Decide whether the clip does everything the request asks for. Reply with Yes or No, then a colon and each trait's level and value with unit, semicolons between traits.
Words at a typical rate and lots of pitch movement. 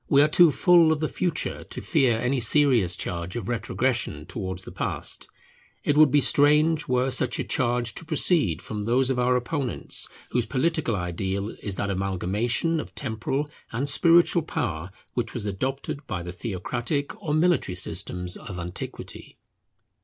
Yes: average, 160 wpm; wide, 7.0 semitones